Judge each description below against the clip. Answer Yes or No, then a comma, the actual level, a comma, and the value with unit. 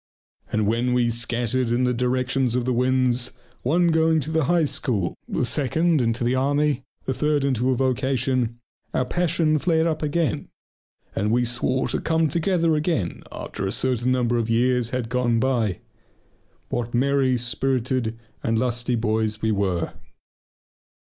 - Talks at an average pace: Yes, average, 155 wpm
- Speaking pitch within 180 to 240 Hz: No, low, 125 Hz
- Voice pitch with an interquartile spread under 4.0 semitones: Yes, average, 3.2 semitones